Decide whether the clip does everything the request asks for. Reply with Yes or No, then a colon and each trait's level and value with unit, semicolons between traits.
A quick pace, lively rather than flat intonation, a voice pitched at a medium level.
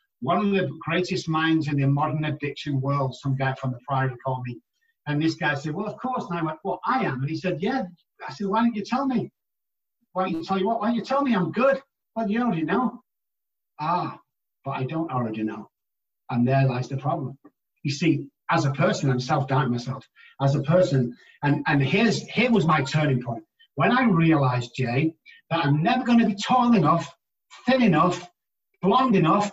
Yes: fast, 210 wpm; wide, 7.0 semitones; medium, 165 Hz